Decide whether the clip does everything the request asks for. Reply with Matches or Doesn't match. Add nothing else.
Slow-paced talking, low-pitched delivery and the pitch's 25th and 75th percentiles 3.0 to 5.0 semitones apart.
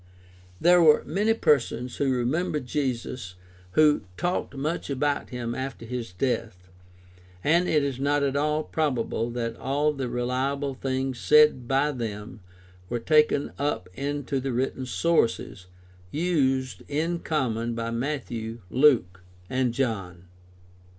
Matches